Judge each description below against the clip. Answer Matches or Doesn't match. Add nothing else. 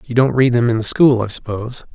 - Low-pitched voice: Matches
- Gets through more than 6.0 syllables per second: Matches